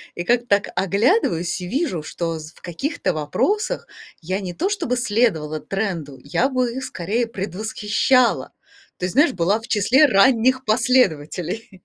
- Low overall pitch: No, high, 205 Hz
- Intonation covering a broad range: Yes, wide, 6.3 semitones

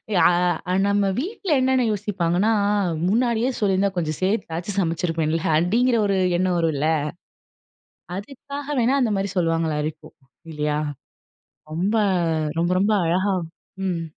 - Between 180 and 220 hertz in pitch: Yes, high, 190 Hz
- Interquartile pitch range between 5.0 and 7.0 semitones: Yes, average, 5.3 semitones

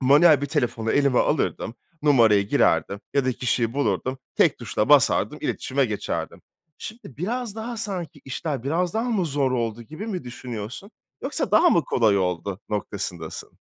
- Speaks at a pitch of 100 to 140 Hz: Yes, low, 135 Hz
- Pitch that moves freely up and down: Yes, wide, 7.1 semitones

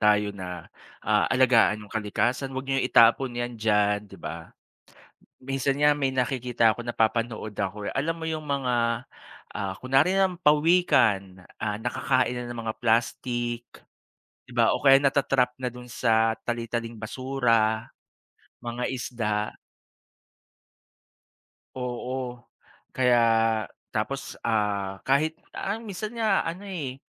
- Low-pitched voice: Yes, low, 120 Hz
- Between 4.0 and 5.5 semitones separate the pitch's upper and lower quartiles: No, average, 3.4 semitones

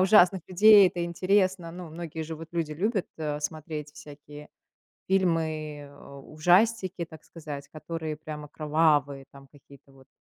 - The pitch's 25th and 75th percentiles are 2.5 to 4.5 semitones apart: Yes, average, 3.2 semitones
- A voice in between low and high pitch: Yes, medium, 160 Hz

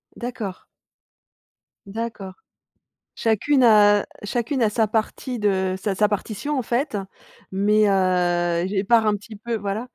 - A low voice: No, high, 210 Hz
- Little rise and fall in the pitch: No, average, 3.0 semitones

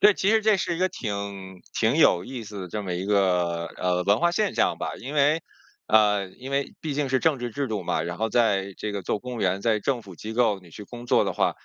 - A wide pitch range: Yes, wide, 6.1 semitones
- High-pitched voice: No, low, 110 Hz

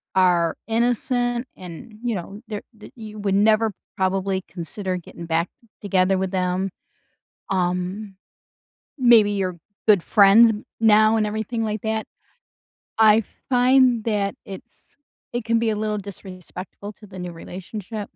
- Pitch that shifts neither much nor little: Yes, average, 3.0 semitones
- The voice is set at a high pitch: Yes, high, 205 Hz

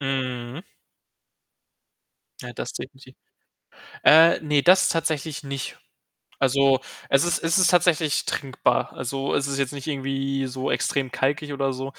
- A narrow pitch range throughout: Yes, narrow, 2.1 semitones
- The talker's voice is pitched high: No, low, 135 Hz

